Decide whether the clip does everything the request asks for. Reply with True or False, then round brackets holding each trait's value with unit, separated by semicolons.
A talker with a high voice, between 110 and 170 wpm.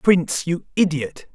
False (165 Hz; 135 wpm)